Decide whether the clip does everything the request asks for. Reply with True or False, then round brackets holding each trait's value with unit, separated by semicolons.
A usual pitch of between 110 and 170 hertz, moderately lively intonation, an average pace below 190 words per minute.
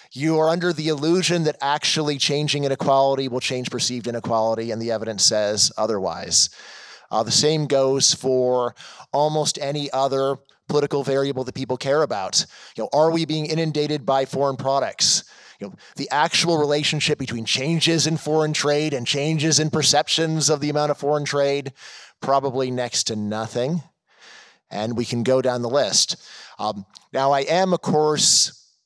True (140 Hz; 3.2 semitones; 160 wpm)